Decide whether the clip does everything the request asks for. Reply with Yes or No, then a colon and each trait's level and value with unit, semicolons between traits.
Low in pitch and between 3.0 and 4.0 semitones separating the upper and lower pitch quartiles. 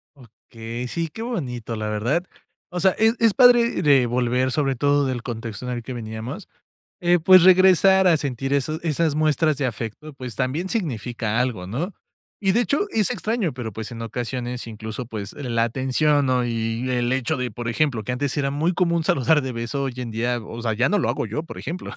No: low, 130 Hz; wide, 5.5 semitones